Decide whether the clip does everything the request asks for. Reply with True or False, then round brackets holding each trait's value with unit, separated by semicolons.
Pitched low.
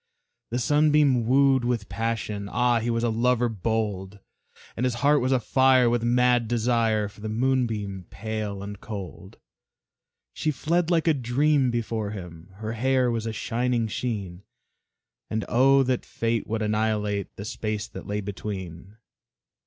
True (115 Hz)